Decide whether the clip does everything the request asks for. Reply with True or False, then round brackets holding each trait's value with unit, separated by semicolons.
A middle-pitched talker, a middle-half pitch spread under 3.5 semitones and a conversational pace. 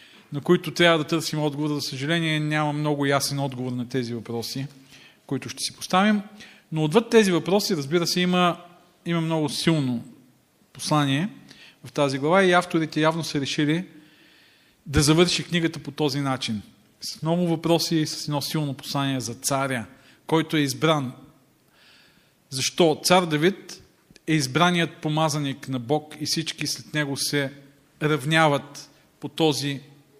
True (150 Hz; 3.0 semitones; 145 wpm)